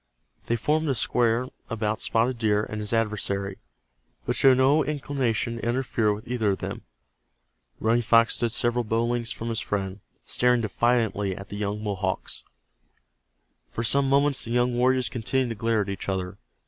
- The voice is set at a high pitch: No, low, 115 Hz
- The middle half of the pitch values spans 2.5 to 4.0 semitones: Yes, average, 2.8 semitones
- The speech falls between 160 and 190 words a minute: Yes, average, 170 wpm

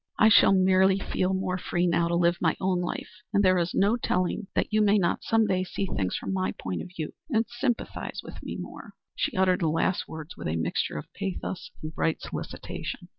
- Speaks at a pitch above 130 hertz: Yes, medium, 185 Hz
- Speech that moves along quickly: Yes, fast, 220 wpm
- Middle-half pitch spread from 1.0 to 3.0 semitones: Yes, average, 2.7 semitones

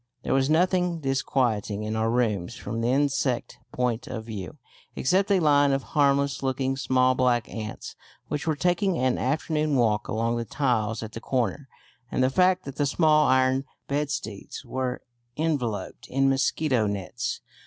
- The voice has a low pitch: Yes, low, 130 Hz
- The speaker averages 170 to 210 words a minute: No, average, 160 wpm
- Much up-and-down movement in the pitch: No, average, 3.9 semitones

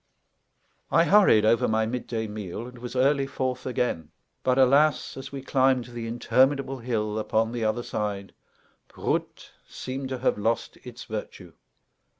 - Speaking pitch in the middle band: No, low, 120 Hz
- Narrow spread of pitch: No, average, 3.2 semitones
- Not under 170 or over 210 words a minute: No, average, 150 wpm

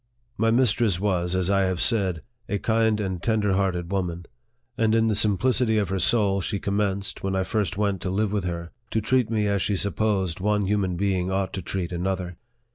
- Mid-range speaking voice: No, low, 100 Hz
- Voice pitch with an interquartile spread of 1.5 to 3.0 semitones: Yes, narrow, 2.4 semitones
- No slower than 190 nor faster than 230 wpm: Yes, average, 200 wpm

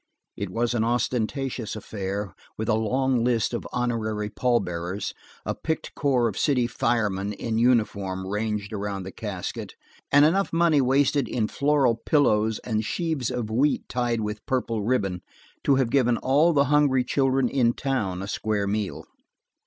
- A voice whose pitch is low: Yes, low, 115 Hz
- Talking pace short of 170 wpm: Yes, average, 155 wpm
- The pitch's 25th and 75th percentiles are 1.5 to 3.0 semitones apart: No, average, 4.0 semitones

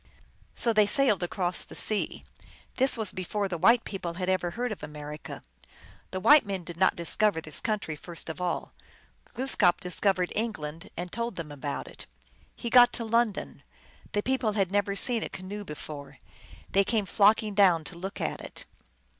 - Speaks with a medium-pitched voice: No, high, 195 Hz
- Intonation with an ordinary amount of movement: Yes, average, 3.9 semitones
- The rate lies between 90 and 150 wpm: No, average, 180 wpm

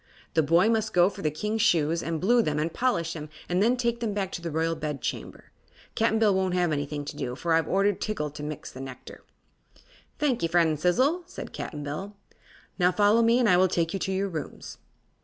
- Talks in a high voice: No, medium, 180 Hz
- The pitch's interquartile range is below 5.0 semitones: No, wide, 5.5 semitones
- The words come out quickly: Yes, fast, 220 wpm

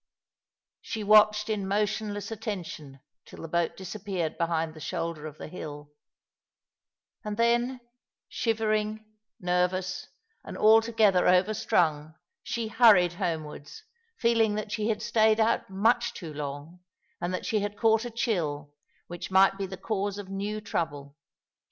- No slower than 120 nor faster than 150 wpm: Yes, average, 140 wpm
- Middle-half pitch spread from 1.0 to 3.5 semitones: No, average, 4.3 semitones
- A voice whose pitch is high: Yes, high, 200 Hz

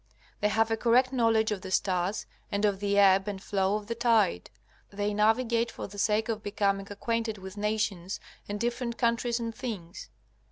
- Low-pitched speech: No, high, 210 Hz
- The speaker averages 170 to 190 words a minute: Yes, average, 185 wpm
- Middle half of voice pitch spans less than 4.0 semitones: Yes, narrow, 2.5 semitones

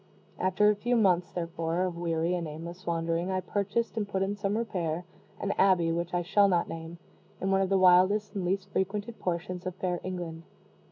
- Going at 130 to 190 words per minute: No, average, 200 wpm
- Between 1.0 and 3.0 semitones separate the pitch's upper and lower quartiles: Yes, narrow, 2.5 semitones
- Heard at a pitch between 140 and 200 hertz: Yes, medium, 185 Hz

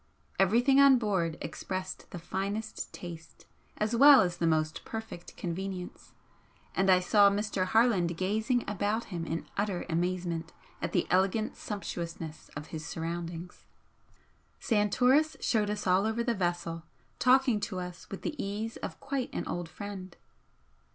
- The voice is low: No, high, 195 Hz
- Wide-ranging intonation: No, average, 4.1 semitones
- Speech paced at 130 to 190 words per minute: Yes, average, 145 wpm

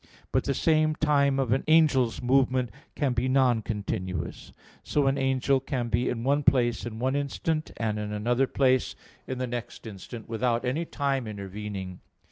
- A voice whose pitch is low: Yes, low, 125 Hz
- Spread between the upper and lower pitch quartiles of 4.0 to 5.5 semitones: No, average, 3.3 semitones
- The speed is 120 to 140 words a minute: No, average, 170 wpm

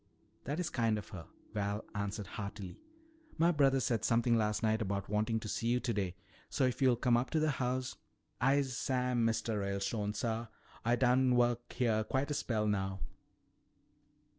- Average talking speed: Yes, average, 175 wpm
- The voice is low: Yes, low, 115 Hz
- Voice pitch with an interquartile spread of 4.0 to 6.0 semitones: No, average, 3.3 semitones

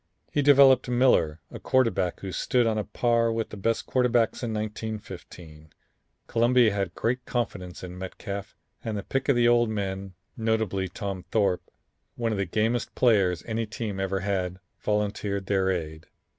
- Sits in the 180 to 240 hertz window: No, low, 105 Hz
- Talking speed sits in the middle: Yes, average, 160 wpm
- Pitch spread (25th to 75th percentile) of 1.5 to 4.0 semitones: Yes, average, 3.6 semitones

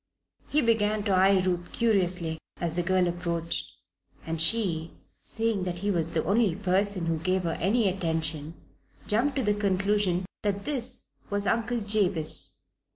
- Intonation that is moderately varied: Yes, average, 3.6 semitones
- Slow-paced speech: No, average, 155 wpm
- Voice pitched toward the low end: No, high, 190 Hz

